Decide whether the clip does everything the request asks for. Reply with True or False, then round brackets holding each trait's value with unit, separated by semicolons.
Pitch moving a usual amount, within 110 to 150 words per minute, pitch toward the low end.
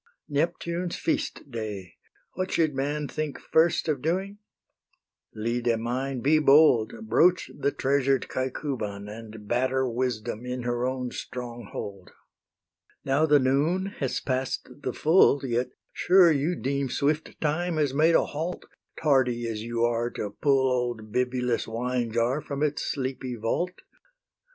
True (4.1 semitones; 135 wpm; 130 Hz)